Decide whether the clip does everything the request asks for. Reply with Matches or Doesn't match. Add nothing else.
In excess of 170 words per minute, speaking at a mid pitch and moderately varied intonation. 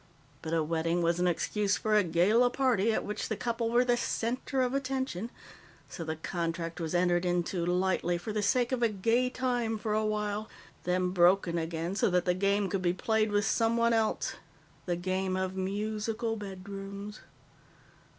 Doesn't match